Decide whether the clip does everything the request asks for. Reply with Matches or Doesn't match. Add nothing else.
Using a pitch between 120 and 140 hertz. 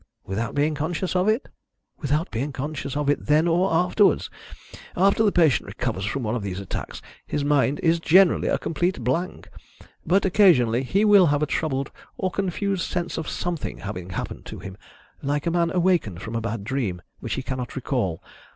Doesn't match